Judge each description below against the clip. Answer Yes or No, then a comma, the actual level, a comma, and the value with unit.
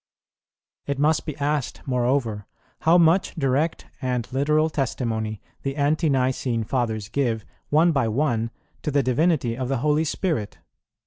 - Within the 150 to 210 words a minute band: No, average, 140 wpm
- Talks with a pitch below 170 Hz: Yes, low, 135 Hz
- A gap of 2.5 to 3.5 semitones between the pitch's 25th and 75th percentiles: No, average, 4.3 semitones